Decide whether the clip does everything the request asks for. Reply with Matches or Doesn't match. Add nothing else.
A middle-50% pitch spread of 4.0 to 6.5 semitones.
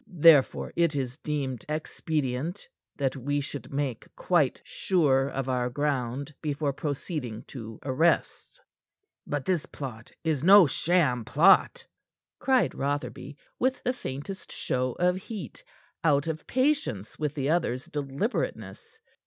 Matches